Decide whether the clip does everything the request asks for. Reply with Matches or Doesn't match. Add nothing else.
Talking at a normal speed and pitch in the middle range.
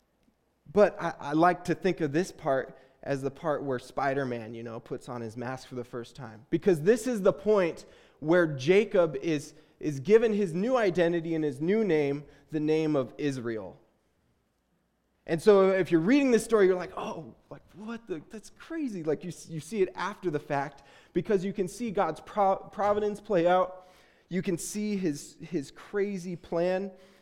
Matches